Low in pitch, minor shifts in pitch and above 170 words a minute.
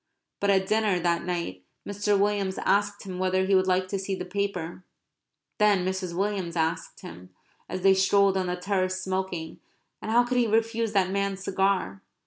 No: high, 190 Hz; narrow, 1.8 semitones; average, 180 wpm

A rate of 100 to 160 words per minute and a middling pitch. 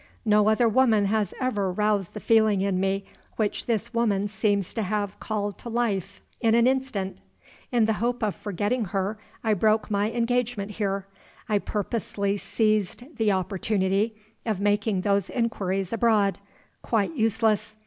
No: average, 150 wpm; high, 210 Hz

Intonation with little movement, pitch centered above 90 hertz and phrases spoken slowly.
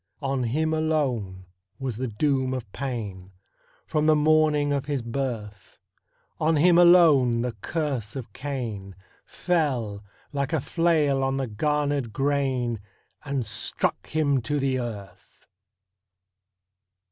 No: average, 4.2 semitones; low, 135 Hz; slow, 125 wpm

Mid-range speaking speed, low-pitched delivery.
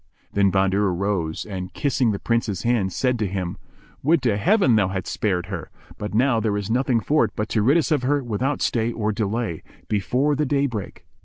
No: fast, 210 wpm; low, 110 Hz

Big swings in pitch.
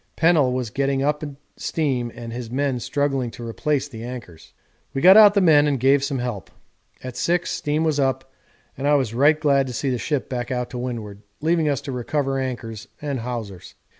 No: average, 3.2 semitones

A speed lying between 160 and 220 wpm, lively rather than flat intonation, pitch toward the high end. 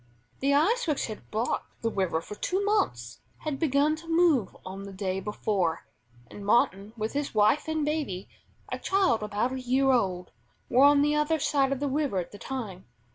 Yes: average, 190 wpm; wide, 6.9 semitones; very high, 255 Hz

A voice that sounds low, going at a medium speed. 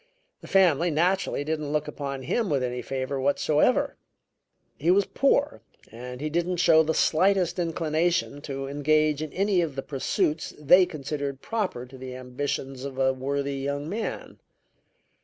No: medium, 150 Hz; average, 155 wpm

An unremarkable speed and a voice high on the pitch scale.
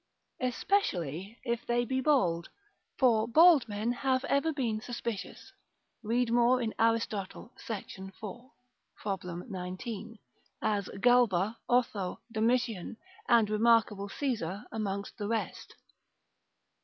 No: slow, 105 wpm; high, 225 Hz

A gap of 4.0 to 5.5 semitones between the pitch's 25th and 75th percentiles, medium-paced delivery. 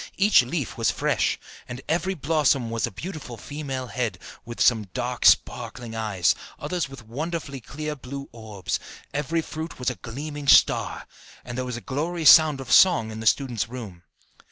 Yes: average, 5.1 semitones; average, 170 wpm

